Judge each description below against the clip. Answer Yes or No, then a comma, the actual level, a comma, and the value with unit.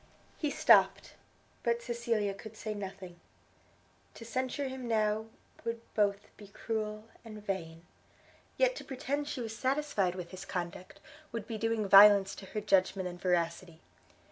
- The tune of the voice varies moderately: Yes, average, 3.4 semitones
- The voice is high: Yes, high, 210 Hz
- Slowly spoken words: No, average, 145 wpm